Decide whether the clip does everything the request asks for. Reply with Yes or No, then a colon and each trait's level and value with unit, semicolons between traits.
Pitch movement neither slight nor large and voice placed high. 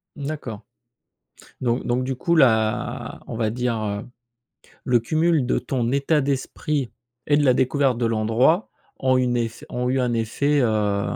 No: average, 3.5 semitones; low, 125 Hz